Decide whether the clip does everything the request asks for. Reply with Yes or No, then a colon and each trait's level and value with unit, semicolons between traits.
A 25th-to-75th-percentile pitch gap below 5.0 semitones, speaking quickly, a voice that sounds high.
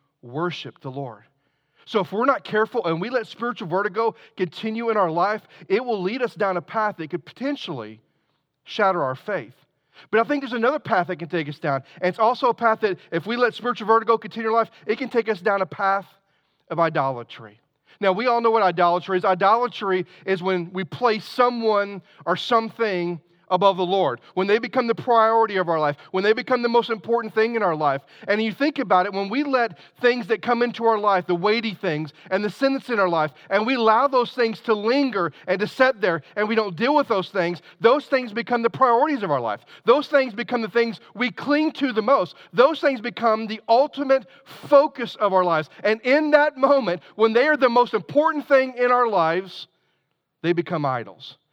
No: wide, 5.5 semitones; fast, 215 wpm; high, 210 Hz